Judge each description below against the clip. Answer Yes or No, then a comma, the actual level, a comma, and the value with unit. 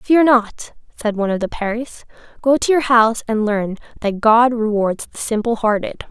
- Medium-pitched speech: No, high, 225 Hz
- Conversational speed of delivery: Yes, average, 185 wpm